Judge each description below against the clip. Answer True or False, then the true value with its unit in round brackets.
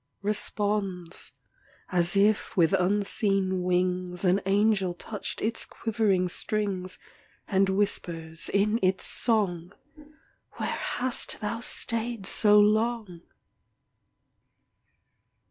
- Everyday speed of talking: False (90 wpm)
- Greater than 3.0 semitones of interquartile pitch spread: False (2.7 semitones)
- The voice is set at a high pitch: True (195 Hz)